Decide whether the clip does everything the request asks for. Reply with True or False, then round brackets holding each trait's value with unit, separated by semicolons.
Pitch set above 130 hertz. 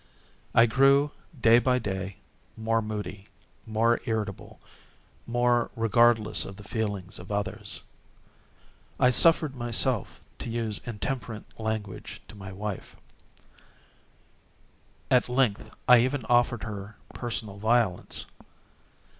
False (115 Hz)